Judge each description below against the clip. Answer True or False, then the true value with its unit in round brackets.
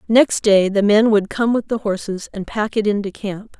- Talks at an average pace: False (250 wpm)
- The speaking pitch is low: False (210 Hz)